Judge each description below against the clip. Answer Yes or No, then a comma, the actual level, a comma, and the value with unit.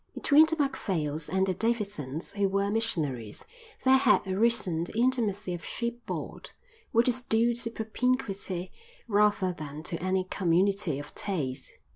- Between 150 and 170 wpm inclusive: No, average, 140 wpm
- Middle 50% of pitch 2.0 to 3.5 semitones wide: No, average, 5.3 semitones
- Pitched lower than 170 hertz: No, high, 200 Hz